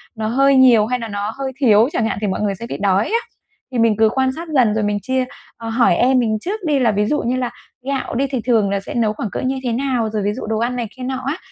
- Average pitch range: Yes, average, 3.4 semitones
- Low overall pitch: No, high, 235 Hz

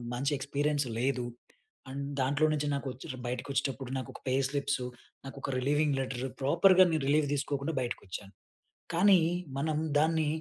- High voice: No, medium, 140 Hz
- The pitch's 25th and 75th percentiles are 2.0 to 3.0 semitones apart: Yes, narrow, 2.4 semitones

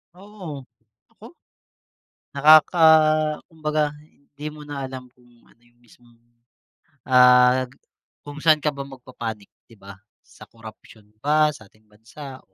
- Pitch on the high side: No, low, 135 Hz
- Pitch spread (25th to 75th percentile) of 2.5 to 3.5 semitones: No, average, 3.9 semitones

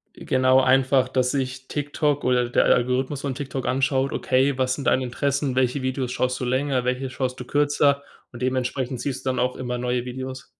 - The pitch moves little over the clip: Yes, narrow, 1.2 semitones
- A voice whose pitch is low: Yes, low, 130 Hz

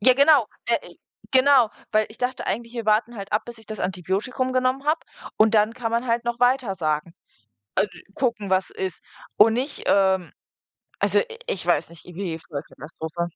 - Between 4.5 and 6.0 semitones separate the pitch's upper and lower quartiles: Yes, average, 5.0 semitones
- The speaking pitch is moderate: No, high, 220 Hz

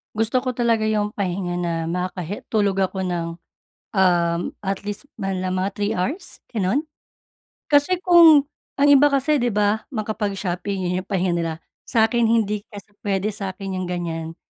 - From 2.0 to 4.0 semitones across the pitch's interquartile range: Yes, average, 3.7 semitones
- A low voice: No, high, 200 Hz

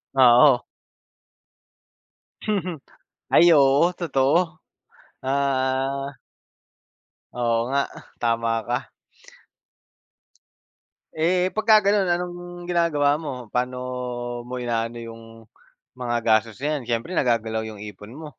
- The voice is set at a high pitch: No, low, 135 Hz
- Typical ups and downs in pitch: No, wide, 5.8 semitones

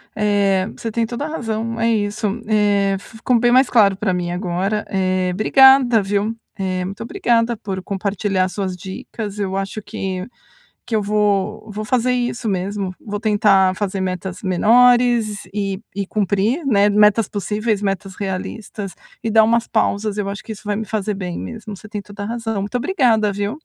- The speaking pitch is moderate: No, high, 205 Hz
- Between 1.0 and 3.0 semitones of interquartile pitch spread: Yes, narrow, 2.4 semitones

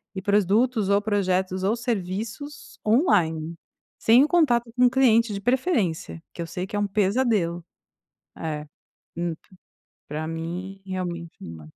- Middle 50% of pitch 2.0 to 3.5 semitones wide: No, average, 5.3 semitones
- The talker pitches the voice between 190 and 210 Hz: Yes, high, 195 Hz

